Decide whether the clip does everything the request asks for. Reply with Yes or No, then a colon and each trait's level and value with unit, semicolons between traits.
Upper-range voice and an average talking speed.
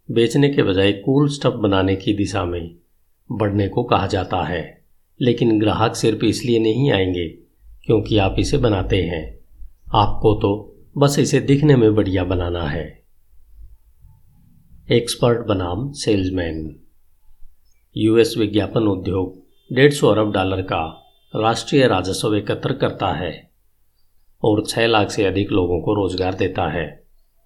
No: low, 105 Hz; average, 130 wpm